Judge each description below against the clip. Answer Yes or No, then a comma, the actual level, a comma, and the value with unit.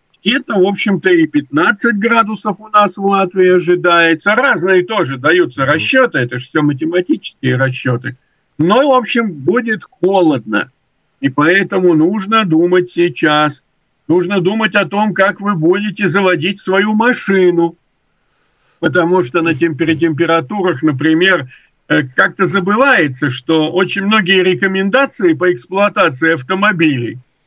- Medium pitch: Yes, medium, 180 Hz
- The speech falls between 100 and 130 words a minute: Yes, average, 120 wpm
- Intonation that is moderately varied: Yes, average, 3.9 semitones